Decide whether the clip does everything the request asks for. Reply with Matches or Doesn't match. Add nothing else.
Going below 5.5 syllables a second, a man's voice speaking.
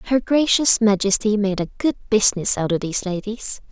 Doesn't match